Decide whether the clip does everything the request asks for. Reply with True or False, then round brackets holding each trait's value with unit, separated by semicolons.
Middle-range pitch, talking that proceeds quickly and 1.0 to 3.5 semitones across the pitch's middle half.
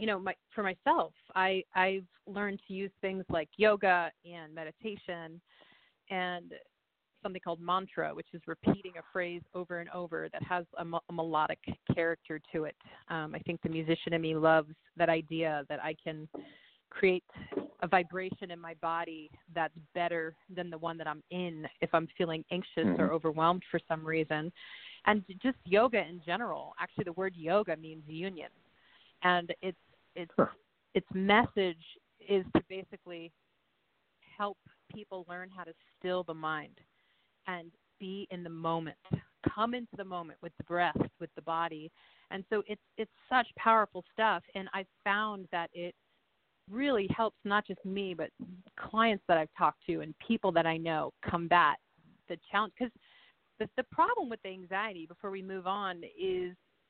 False (180 Hz; 165 wpm; 3.2 semitones)